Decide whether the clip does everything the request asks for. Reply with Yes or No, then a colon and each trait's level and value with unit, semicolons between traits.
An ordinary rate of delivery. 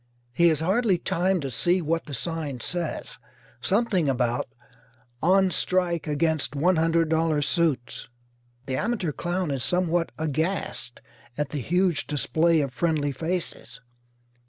No: slow, 125 wpm